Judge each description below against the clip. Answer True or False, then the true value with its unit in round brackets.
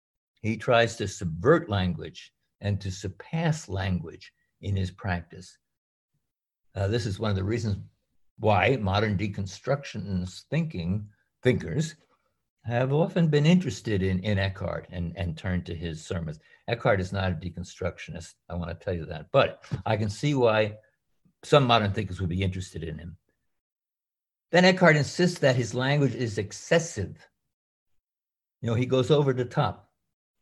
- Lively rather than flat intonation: True (5.8 semitones)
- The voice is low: True (105 Hz)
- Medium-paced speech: True (150 wpm)